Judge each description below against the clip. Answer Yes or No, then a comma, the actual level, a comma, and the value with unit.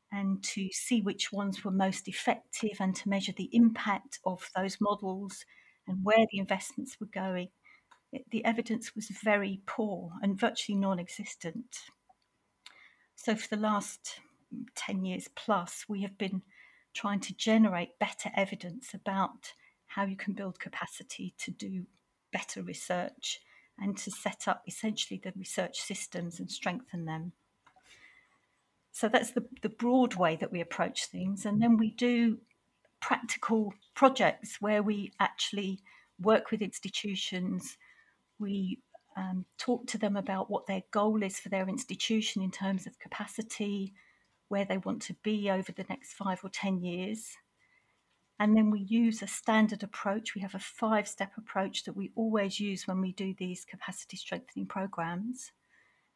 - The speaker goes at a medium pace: Yes, average, 155 wpm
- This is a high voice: Yes, high, 200 Hz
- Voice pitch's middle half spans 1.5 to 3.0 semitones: Yes, narrow, 2.6 semitones